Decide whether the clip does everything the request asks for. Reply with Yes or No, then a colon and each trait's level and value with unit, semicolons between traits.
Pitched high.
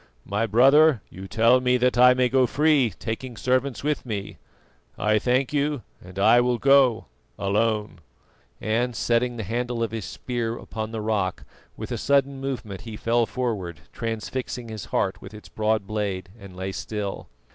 No: low, 115 Hz